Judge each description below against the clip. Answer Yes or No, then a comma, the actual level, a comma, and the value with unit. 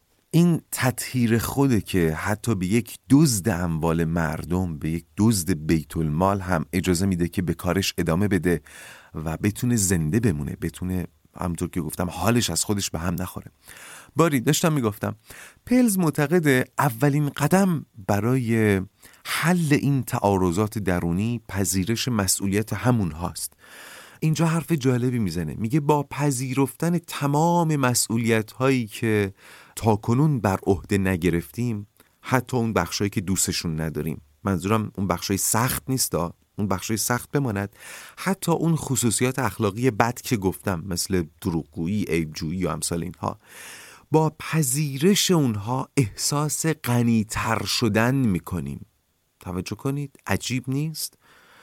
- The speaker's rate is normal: Yes, average, 125 wpm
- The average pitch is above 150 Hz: No, low, 105 Hz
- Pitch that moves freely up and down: Yes, wide, 6.3 semitones